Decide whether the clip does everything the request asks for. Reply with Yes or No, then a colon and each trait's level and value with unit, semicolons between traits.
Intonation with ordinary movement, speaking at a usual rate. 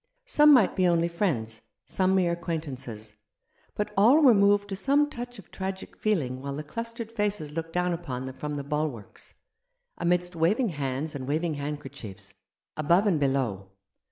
No: wide, 6.4 semitones; average, 160 wpm